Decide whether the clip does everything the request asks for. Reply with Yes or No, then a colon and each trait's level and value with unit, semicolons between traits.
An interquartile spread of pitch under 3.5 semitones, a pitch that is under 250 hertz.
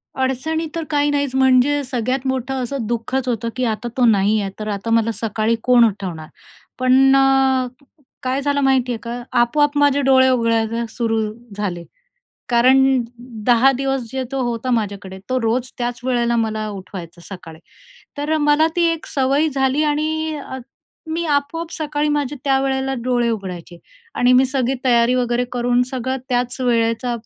No: average, 2.8 semitones; very high, 255 Hz